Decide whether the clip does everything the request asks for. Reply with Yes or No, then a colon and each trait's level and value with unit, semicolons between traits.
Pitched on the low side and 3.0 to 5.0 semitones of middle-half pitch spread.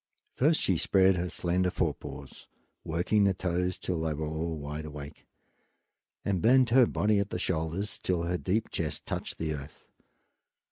Yes: very low, 90 Hz; average, 3.8 semitones